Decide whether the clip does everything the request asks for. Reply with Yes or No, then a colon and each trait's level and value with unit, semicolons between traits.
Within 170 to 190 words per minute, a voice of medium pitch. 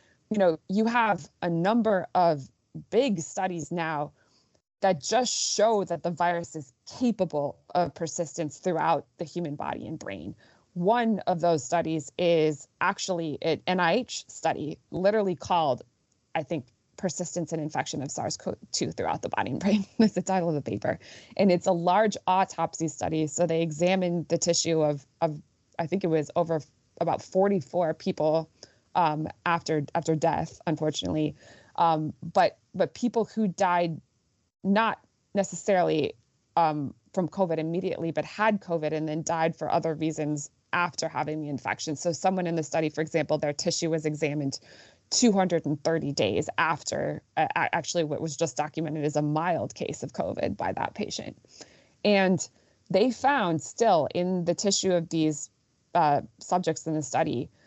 No: average, 155 wpm; medium, 165 Hz